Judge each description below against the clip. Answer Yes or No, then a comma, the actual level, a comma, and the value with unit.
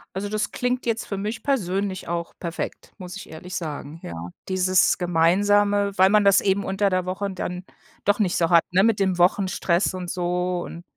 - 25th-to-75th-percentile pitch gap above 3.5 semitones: No, narrow, 2.4 semitones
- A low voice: No, medium, 185 Hz